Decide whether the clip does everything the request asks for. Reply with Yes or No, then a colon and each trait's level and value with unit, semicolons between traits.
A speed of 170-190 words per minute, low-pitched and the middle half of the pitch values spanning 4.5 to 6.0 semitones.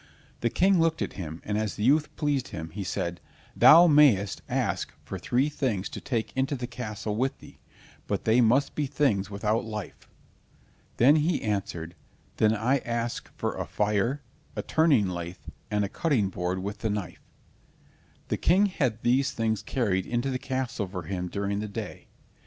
Yes: average, 175 wpm; low, 115 Hz; average, 5.2 semitones